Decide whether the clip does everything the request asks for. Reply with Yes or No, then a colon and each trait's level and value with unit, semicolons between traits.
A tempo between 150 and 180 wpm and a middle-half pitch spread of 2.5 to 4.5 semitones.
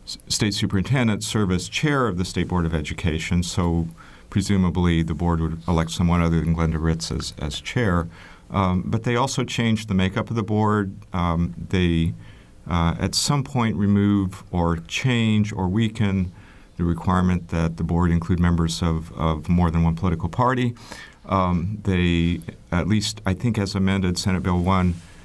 Yes: average, 170 wpm; average, 3.5 semitones